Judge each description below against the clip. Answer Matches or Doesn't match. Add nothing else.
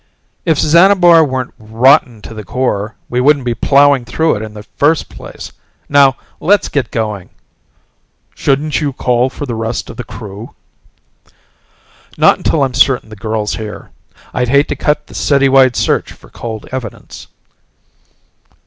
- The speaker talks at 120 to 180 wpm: Matches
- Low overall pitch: Matches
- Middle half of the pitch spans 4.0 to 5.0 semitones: Matches